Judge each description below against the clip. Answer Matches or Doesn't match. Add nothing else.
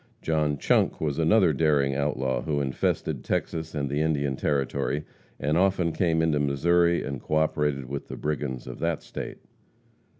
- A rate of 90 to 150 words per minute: Doesn't match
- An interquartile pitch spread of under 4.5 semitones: Matches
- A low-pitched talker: Matches